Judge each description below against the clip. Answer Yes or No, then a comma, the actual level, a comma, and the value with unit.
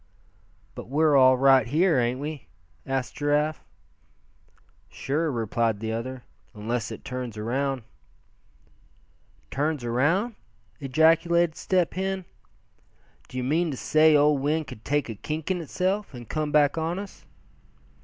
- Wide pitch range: No, average, 4.0 semitones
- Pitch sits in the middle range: Yes, medium, 145 Hz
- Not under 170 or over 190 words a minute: No, slow, 135 wpm